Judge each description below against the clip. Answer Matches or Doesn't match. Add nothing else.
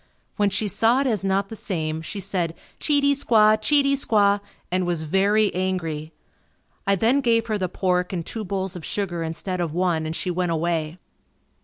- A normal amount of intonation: Matches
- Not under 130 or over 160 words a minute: Doesn't match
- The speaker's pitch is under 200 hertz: Matches